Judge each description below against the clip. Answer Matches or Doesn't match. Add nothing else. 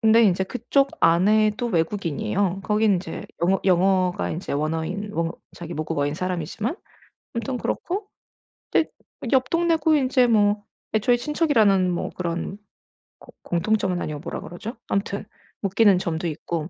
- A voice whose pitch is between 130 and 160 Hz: Doesn't match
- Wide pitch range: Doesn't match